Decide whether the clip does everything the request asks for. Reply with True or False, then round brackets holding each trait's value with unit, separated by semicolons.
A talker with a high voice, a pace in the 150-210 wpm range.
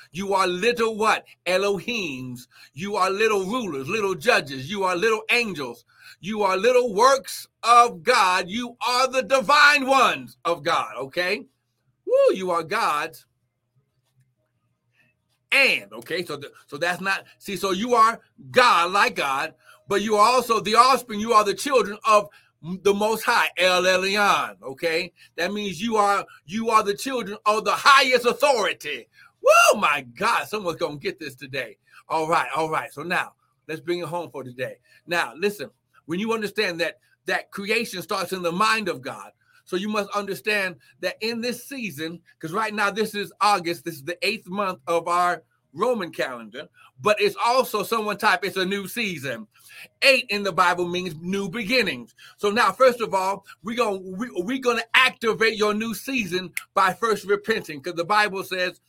True (200 Hz; 175 wpm)